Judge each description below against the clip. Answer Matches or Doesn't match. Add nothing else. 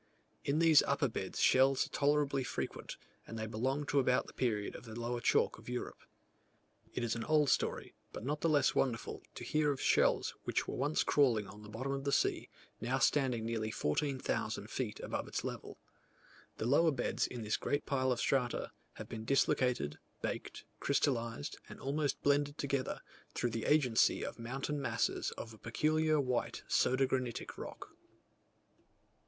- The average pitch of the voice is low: Matches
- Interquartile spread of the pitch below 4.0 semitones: Matches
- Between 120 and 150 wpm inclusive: Doesn't match